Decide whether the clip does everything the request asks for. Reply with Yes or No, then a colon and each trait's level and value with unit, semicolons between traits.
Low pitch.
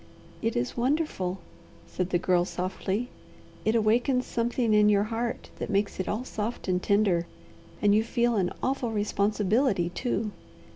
No: high, 215 Hz